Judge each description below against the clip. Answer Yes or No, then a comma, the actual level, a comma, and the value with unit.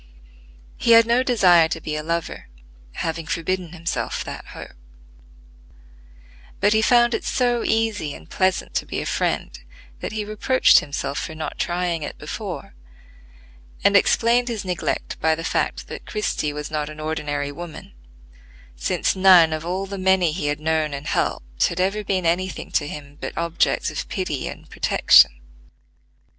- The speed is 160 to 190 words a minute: Yes, average, 165 wpm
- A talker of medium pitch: Yes, medium, 170 Hz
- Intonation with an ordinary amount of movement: Yes, average, 4.7 semitones